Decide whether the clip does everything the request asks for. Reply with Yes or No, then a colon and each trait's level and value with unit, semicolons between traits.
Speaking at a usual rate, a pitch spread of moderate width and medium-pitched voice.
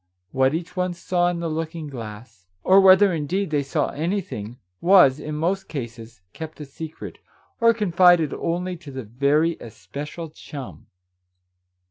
Yes: average, 145 wpm; average, 4.7 semitones; medium, 160 Hz